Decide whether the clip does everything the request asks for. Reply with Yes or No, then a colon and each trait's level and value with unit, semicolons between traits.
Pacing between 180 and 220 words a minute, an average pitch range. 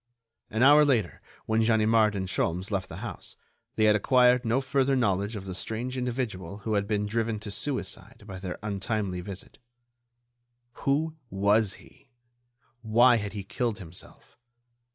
No: average, 155 wpm; average, 3.8 semitones